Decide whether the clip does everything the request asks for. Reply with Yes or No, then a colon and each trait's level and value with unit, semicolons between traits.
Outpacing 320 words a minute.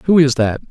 No: fast, 255 wpm